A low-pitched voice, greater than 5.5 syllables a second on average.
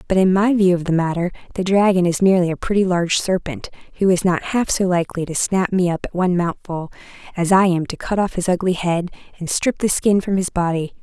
No: medium, 185 Hz; 6.0 syllables/s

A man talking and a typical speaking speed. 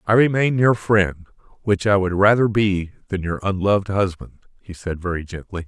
Yes: male; average, 180 wpm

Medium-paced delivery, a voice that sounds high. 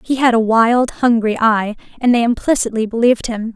Yes: average, 185 wpm; high, 230 Hz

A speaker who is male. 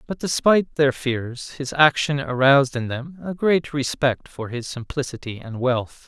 Yes: male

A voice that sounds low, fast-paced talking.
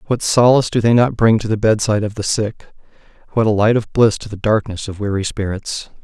Yes: low, 110 Hz; fast, 230 wpm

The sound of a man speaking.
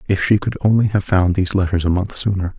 Yes: male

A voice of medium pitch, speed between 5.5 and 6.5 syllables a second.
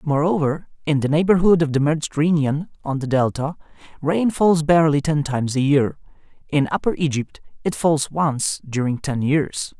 No: medium, 150 Hz; 5.1 syllables/s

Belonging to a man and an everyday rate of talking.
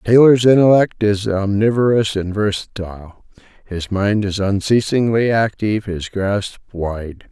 No: male; slow, 105 wpm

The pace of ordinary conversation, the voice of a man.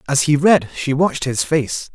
No: fast, 215 wpm; male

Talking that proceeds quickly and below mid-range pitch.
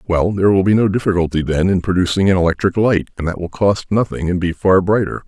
Yes: fast, 240 wpm; very low, 95 Hz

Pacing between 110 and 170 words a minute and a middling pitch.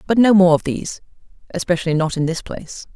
No: fast, 205 wpm; medium, 180 Hz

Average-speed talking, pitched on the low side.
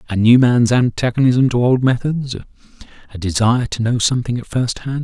Yes: average, 180 wpm; low, 120 Hz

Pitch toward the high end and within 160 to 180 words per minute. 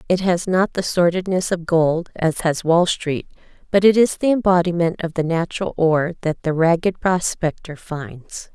No: medium, 170 Hz; average, 175 wpm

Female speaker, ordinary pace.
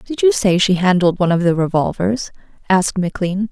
Yes: female; average, 190 wpm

